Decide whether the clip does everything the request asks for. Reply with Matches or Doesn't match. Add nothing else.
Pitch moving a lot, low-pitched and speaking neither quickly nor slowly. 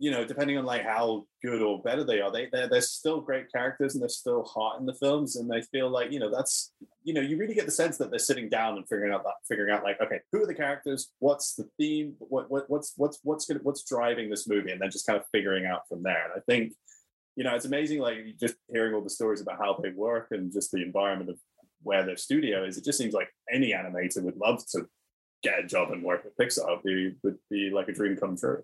Doesn't match